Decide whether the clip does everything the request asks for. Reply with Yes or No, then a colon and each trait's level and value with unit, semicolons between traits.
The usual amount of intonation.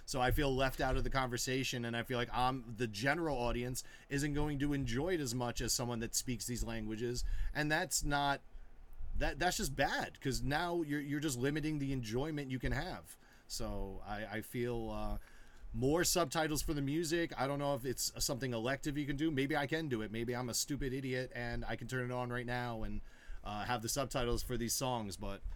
Yes: average, 3.4 semitones